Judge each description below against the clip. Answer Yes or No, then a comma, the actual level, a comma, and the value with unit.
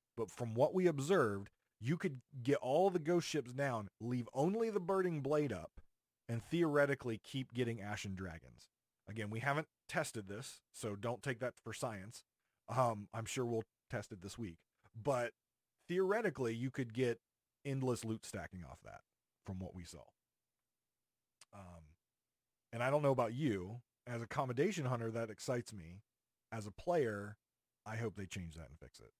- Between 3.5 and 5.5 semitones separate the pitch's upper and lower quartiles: Yes, average, 4.8 semitones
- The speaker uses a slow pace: No, average, 170 wpm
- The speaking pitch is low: Yes, low, 120 Hz